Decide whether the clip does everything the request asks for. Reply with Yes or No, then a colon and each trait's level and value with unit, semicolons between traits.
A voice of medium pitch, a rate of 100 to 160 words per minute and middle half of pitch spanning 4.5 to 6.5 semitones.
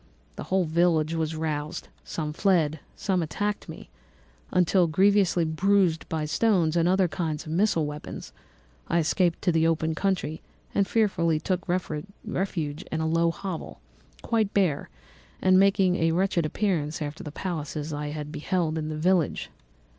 No: medium, 165 Hz; average, 155 wpm; average, 3.2 semitones